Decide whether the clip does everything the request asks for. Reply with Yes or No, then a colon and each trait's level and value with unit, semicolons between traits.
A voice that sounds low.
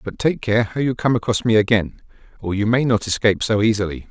Yes: low, 110 Hz